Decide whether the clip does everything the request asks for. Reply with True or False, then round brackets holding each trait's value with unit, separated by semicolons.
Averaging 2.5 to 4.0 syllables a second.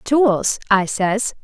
True (2.6 syllables/s)